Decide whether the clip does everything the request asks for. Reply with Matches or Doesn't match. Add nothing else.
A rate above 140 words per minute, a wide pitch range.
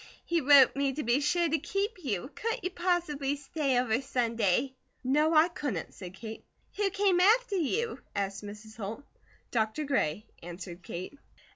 Matches